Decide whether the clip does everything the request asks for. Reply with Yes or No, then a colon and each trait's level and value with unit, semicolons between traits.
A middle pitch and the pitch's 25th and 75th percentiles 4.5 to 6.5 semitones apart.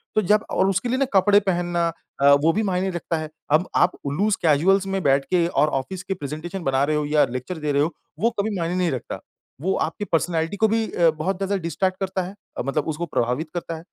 No: medium, 175 Hz; average, 4.1 semitones